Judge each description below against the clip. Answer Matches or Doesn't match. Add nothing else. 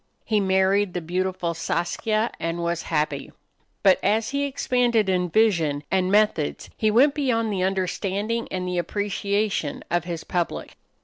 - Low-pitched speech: Doesn't match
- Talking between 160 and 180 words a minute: Doesn't match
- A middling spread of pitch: Matches